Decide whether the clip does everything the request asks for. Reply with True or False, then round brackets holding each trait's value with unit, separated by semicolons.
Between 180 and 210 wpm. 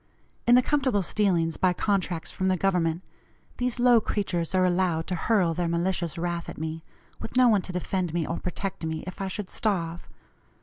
True (190 wpm)